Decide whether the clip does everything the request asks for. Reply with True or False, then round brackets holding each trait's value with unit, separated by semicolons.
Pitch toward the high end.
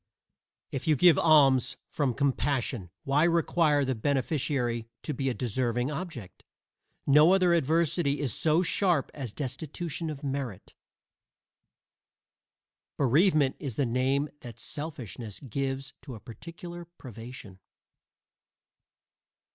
False (140 Hz)